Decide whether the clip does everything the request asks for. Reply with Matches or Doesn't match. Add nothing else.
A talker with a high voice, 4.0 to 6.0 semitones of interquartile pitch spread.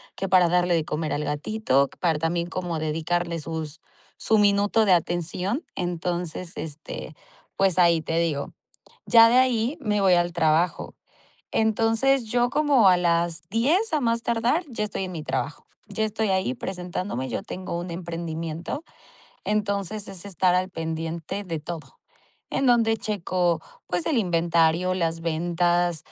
Doesn't match